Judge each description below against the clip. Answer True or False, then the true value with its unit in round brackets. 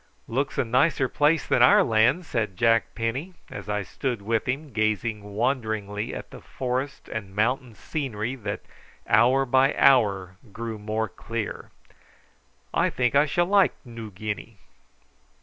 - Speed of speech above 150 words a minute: False (145 wpm)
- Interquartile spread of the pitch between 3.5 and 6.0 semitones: True (3.9 semitones)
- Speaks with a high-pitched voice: False (115 Hz)